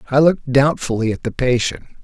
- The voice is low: Yes, low, 130 Hz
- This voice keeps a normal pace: Yes, average, 175 wpm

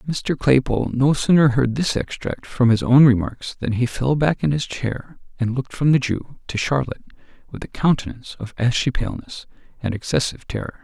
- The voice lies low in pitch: Yes, low, 130 Hz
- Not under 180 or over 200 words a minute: Yes, average, 190 wpm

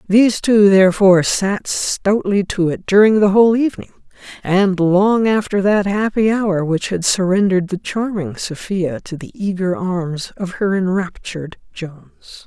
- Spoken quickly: No, average, 150 wpm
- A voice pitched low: No, high, 190 Hz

